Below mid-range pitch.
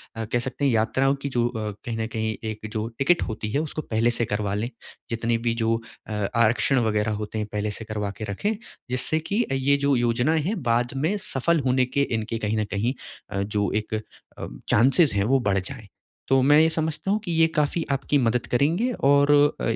Yes: low, 120 Hz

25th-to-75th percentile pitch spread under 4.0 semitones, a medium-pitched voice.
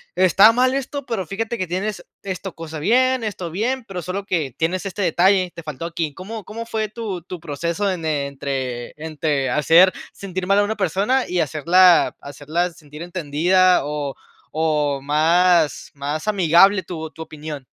No: average, 4.3 semitones; medium, 175 Hz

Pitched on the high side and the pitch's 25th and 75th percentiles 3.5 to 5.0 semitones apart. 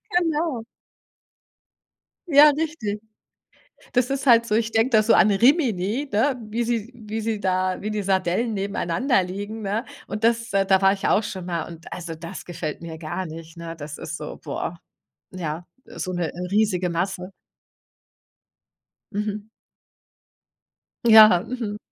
Yes: high, 205 Hz; average, 4.3 semitones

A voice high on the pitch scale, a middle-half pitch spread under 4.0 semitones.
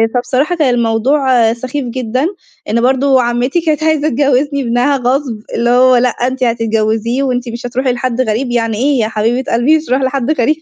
Yes: very high, 250 Hz; narrow, 2.5 semitones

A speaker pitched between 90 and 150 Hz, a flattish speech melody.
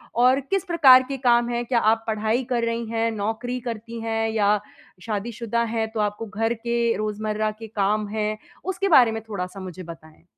No: high, 225 Hz; narrow, 2.0 semitones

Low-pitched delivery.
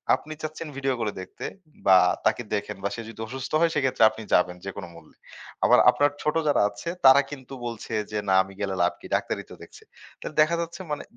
Yes: low, 125 Hz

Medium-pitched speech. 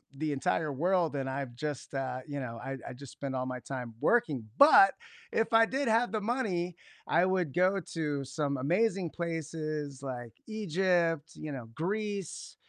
Yes: medium, 155 Hz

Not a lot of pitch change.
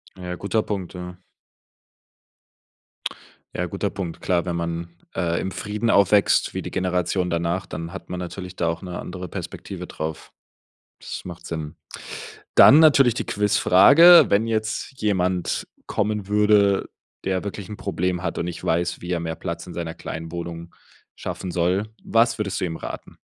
No: average, 3.1 semitones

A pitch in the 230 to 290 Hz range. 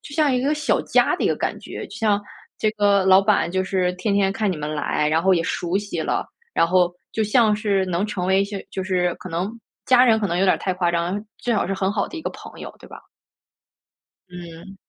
No: high, 195 Hz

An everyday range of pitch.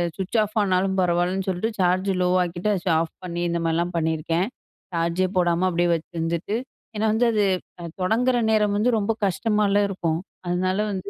Yes: average, 3.0 semitones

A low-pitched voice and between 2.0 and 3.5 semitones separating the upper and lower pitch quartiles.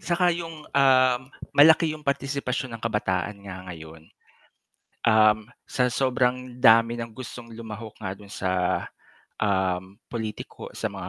No: low, 115 Hz; average, 4.4 semitones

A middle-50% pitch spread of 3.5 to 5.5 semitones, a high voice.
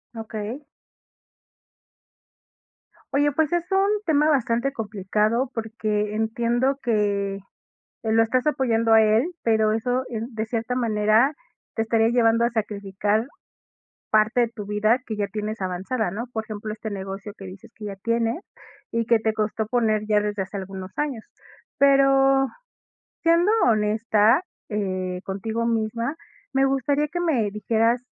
No: average, 2.8 semitones; high, 225 Hz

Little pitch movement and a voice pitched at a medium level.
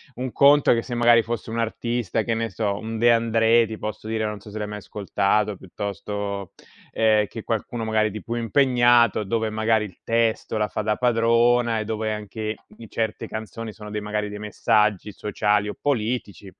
No: narrow, 1.7 semitones; low, 110 Hz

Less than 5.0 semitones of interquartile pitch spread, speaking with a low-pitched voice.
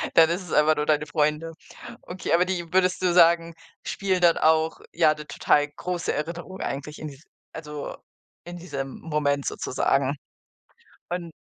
No: narrow, 2.6 semitones; medium, 160 Hz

